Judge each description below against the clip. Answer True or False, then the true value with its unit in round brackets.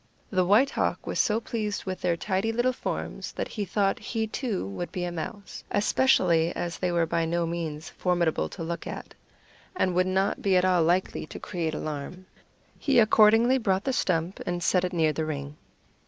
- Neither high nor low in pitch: True (180 Hz)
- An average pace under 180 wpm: False (195 wpm)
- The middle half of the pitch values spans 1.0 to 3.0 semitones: False (3.9 semitones)